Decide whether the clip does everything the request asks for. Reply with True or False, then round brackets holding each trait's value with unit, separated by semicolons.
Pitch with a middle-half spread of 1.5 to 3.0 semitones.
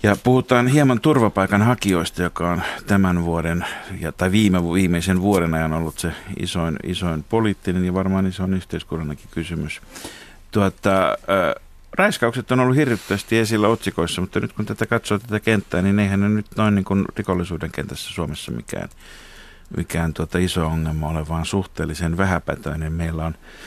False (3.7 semitones)